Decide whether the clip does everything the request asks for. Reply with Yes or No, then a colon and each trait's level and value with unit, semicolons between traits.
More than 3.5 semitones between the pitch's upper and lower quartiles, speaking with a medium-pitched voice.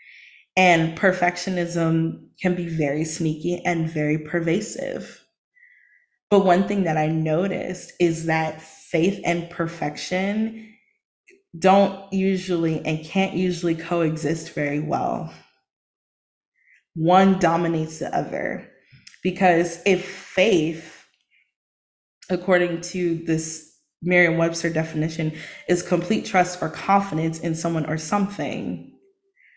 No: average, 2.7 semitones; medium, 170 Hz